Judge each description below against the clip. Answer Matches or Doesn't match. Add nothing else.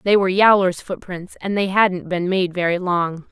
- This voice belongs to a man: Doesn't match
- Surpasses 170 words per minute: Matches